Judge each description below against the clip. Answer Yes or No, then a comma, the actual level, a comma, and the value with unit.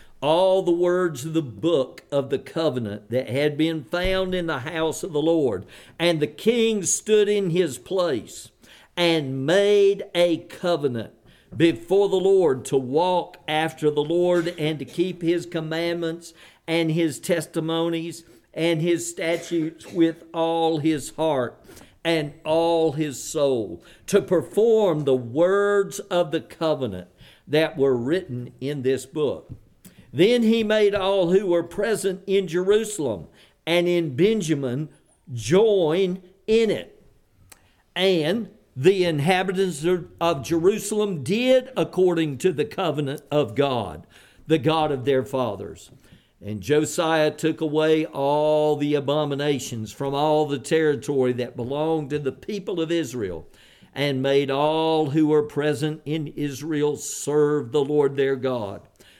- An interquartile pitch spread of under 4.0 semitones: Yes, average, 3.5 semitones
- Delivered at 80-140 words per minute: Yes, slow, 135 wpm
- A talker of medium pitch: Yes, medium, 160 Hz